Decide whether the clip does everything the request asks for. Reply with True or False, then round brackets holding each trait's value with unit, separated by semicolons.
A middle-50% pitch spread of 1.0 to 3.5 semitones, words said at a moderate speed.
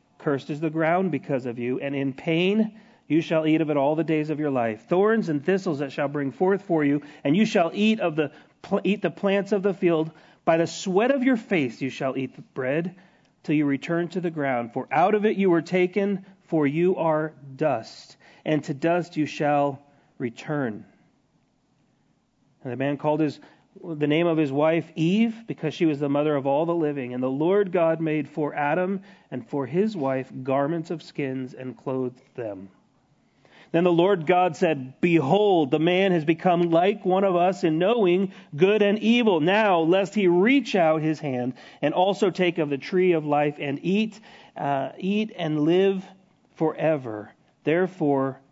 False (4.5 semitones; 190 wpm)